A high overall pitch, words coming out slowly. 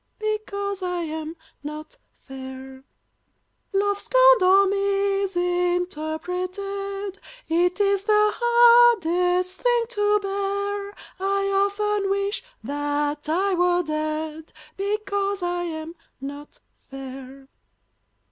Yes: very high, 385 Hz; slow, 90 wpm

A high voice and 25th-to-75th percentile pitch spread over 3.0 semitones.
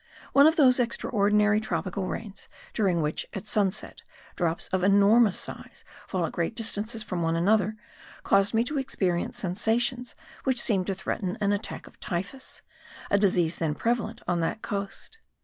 Yes: high, 200 Hz; average, 3.8 semitones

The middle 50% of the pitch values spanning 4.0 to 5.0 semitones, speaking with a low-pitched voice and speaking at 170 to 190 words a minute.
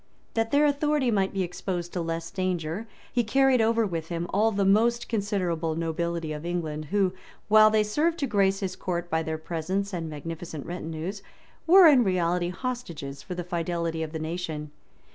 No: average, 4.6 semitones; medium, 180 Hz; average, 180 wpm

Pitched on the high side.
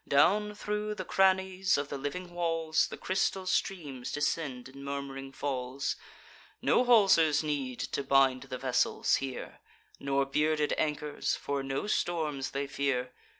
No: medium, 145 Hz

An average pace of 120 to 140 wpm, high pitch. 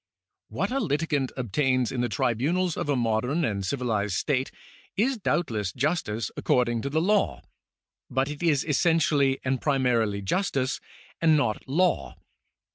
No: slow, 135 wpm; low, 135 Hz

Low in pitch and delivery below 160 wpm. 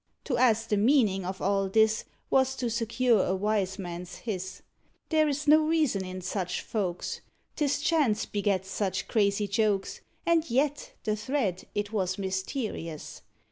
No: high, 210 Hz; average, 150 wpm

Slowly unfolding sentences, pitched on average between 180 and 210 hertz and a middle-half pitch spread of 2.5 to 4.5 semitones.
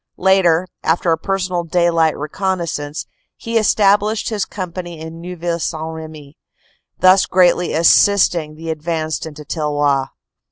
No: slow, 125 wpm; medium, 170 Hz; average, 2.8 semitones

